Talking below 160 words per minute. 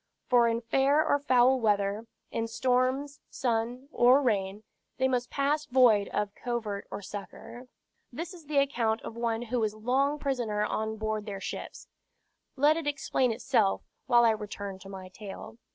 No: average, 165 wpm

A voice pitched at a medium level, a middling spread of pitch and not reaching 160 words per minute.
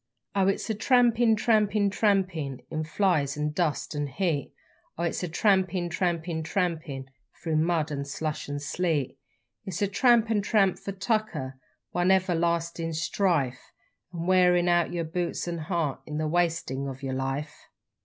No: medium, 170 Hz; average, 4.0 semitones; average, 165 wpm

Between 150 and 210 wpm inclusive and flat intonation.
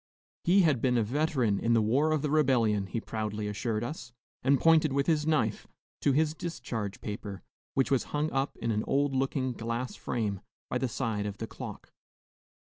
No: average, 190 wpm; average, 5.1 semitones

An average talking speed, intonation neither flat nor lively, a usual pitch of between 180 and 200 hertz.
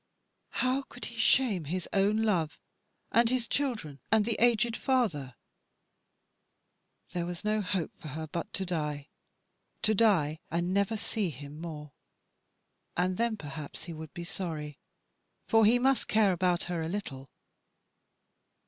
No: average, 150 wpm; wide, 5.9 semitones; medium, 185 Hz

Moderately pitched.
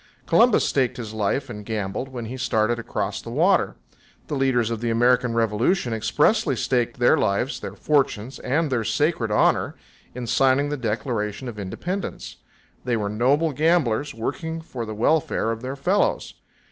No: low, 125 Hz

